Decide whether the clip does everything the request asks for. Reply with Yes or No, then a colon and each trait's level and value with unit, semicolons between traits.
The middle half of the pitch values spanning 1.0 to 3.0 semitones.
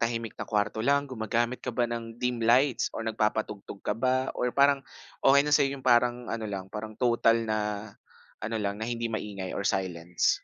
Yes: narrow, 2.6 semitones